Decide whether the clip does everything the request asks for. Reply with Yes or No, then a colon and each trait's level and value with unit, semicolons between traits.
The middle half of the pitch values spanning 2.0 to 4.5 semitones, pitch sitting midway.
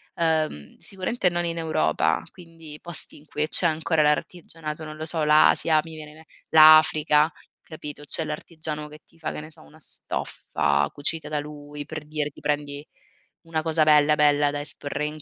No: narrow, 1.4 semitones; medium, 155 Hz